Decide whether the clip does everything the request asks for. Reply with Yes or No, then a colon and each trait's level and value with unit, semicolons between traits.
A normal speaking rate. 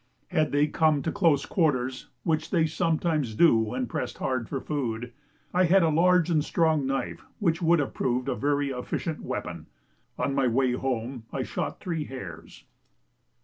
Yes: average, 170 wpm